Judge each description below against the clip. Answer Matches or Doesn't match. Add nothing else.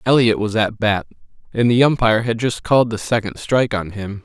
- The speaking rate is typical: Doesn't match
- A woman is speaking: Doesn't match